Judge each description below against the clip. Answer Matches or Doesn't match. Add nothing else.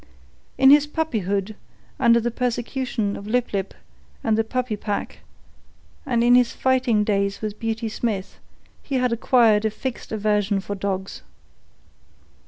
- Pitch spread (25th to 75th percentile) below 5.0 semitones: Matches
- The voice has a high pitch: Matches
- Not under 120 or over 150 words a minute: Matches